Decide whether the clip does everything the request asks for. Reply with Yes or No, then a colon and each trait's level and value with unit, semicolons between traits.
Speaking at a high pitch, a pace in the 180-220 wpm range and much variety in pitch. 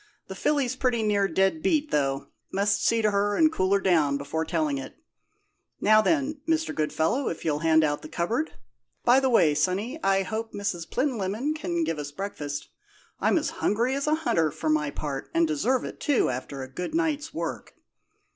Yes: high, 200 Hz; average, 190 wpm; wide, 8.8 semitones